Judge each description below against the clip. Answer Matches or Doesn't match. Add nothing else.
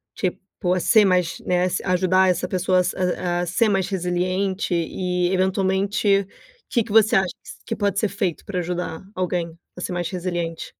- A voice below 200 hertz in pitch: Matches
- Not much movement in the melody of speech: Matches